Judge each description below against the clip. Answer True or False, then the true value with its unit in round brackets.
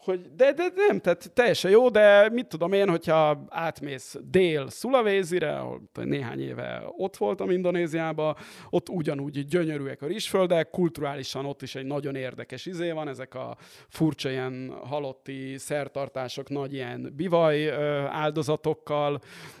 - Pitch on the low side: False (155 Hz)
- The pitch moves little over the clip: False (4.6 semitones)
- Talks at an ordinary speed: True (135 wpm)